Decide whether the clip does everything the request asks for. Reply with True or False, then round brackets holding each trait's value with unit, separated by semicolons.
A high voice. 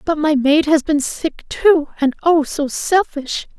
True (305 Hz)